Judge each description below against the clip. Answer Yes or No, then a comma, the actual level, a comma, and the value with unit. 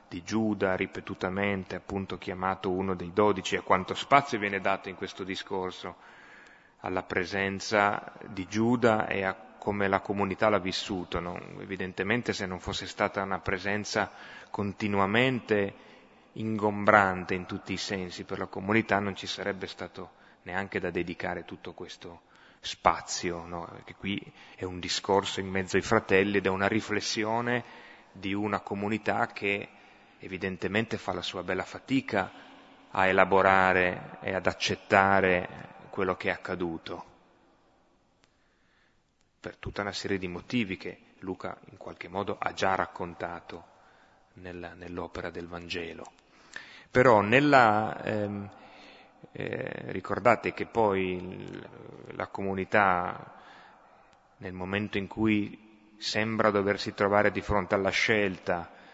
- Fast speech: No, average, 125 wpm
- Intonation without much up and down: Yes, narrow, 2.0 semitones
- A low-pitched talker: Yes, low, 100 Hz